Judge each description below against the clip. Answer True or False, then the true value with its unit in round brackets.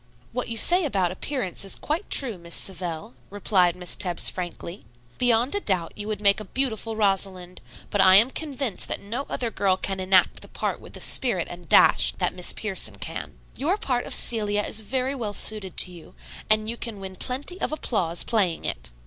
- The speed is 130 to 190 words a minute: False (200 wpm)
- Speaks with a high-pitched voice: True (205 Hz)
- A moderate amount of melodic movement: True (4.9 semitones)